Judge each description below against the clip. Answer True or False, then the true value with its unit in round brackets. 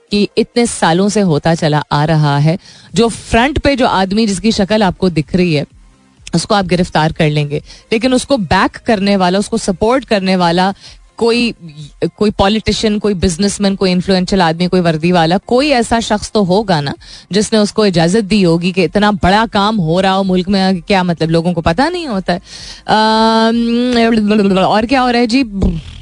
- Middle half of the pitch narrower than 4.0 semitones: False (4.3 semitones)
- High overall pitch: True (195 Hz)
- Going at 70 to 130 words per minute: False (175 wpm)